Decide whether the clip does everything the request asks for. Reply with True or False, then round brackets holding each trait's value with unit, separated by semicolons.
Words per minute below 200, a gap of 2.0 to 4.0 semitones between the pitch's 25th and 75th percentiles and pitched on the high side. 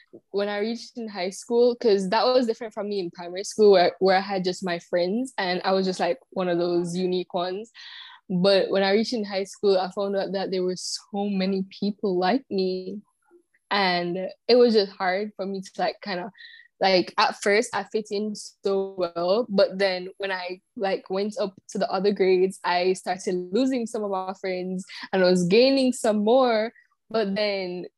False (205 wpm; 2.8 semitones; 195 Hz)